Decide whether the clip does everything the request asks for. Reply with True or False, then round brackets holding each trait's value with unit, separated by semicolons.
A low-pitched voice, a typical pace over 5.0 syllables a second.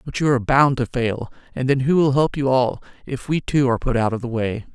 True (130 Hz; 5.8 syllables/s)